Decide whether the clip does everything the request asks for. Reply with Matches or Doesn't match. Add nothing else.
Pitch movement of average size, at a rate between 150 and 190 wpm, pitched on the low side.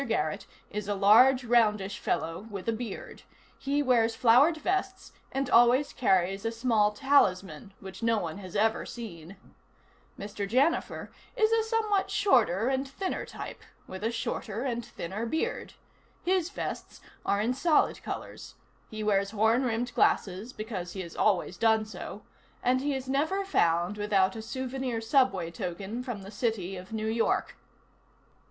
Doesn't match